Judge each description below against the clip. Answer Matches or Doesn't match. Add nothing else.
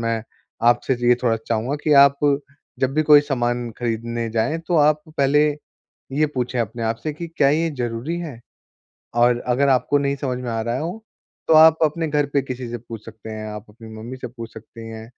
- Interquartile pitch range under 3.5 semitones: Doesn't match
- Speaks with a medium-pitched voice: Doesn't match